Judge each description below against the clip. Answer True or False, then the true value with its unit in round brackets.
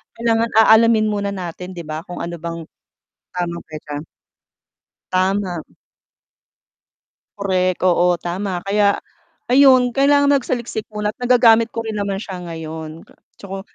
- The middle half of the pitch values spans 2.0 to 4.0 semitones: False (4.5 semitones)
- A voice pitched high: True (195 Hz)